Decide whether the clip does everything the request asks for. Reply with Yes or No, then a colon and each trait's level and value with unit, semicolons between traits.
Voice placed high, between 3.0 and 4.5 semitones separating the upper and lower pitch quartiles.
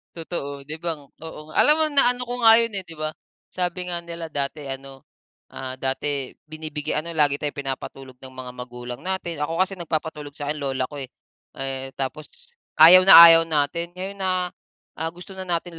No: medium, 155 Hz; average, 4.1 semitones